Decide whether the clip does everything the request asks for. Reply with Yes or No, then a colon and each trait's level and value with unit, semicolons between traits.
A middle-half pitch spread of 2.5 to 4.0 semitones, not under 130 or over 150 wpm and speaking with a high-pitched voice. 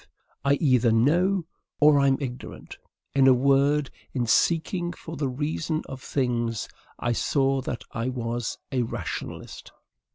No: average, 3.3 semitones; slow, 135 wpm; low, 135 Hz